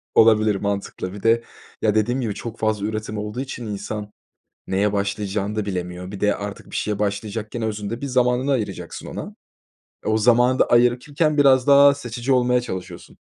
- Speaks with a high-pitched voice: No, low, 110 Hz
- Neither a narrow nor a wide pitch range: Yes, average, 3.2 semitones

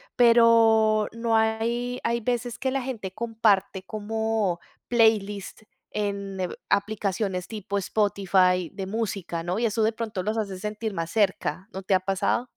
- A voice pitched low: No, high, 215 Hz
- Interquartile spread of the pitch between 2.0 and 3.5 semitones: Yes, average, 2.7 semitones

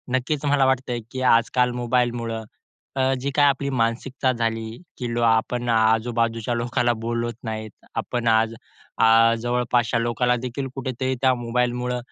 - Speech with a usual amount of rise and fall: No, narrow, 1.8 semitones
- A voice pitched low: Yes, low, 120 Hz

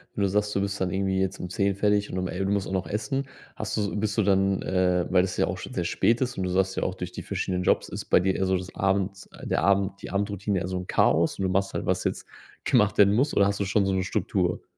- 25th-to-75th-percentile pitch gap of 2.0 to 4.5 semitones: No, narrow, 1.4 semitones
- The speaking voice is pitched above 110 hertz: No, very low, 95 Hz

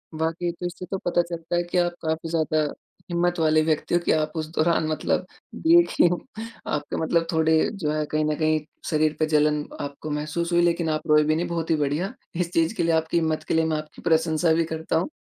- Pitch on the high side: No, medium, 160 Hz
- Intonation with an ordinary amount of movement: No, narrow, 1.8 semitones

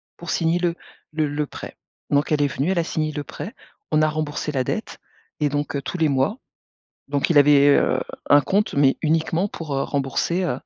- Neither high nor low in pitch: Yes, medium, 150 Hz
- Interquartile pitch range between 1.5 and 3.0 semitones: Yes, narrow, 2.4 semitones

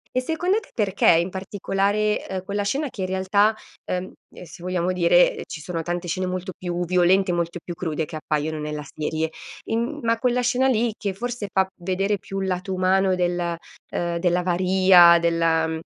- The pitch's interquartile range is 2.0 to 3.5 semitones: Yes, average, 2.8 semitones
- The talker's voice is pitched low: No, medium, 185 Hz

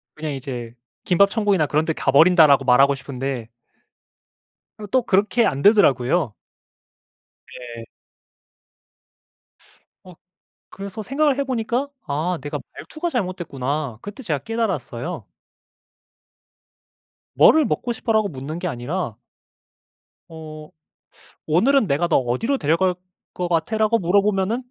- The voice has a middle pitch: Yes, medium, 175 Hz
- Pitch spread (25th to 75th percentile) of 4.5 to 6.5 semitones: No, wide, 7.6 semitones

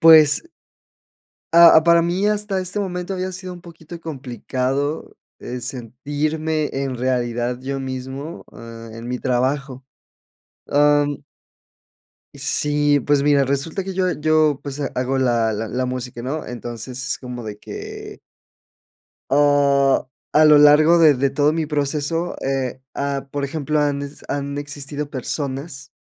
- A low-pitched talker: No, medium, 145 Hz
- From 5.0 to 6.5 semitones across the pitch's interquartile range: No, average, 3.3 semitones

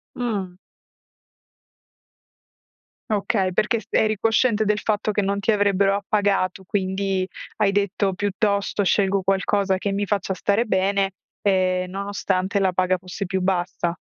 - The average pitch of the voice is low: No, high, 195 Hz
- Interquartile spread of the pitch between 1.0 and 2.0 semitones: Yes, narrow, 1.5 semitones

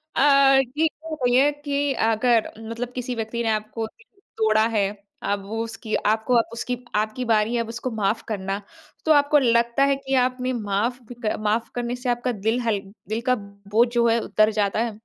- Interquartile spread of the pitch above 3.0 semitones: No, narrow, 2.5 semitones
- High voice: Yes, high, 230 Hz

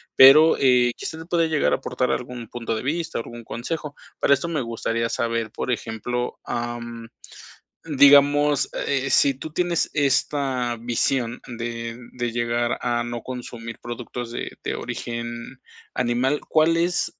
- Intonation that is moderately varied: Yes, average, 3.2 semitones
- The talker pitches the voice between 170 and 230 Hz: No, low, 125 Hz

